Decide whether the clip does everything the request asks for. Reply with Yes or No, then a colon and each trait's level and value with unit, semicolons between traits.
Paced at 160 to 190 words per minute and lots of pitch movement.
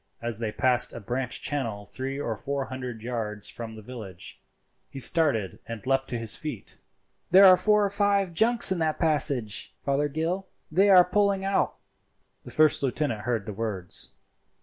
Yes: average, 170 wpm; wide, 7.2 semitones